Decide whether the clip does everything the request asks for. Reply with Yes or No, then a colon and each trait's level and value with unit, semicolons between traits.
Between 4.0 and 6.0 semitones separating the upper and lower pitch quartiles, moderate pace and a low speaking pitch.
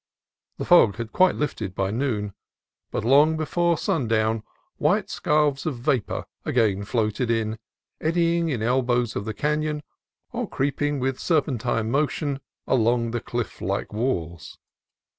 No: average, 5.1 semitones; slow, 130 wpm; low, 125 Hz